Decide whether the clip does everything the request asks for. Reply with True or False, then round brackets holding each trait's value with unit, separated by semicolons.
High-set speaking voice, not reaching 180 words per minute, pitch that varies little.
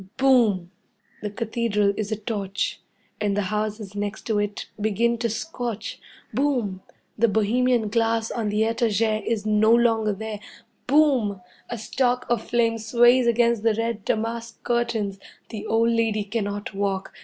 True (220 Hz; 145 wpm; 2.2 semitones)